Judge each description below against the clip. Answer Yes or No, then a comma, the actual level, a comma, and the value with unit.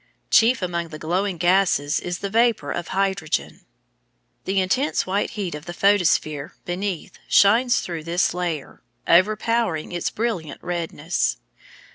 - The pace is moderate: No, slow, 130 wpm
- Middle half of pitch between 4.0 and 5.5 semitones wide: No, average, 3.4 semitones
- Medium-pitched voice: Yes, medium, 180 Hz